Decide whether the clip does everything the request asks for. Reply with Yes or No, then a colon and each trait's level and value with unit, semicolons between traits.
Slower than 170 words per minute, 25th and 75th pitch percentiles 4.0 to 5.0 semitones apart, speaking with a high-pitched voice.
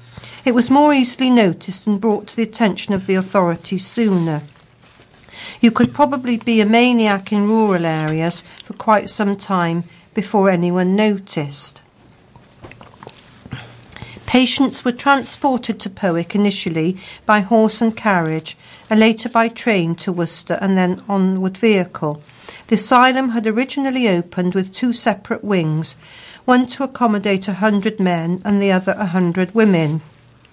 Yes: average, 140 wpm; average, 4.5 semitones; high, 205 Hz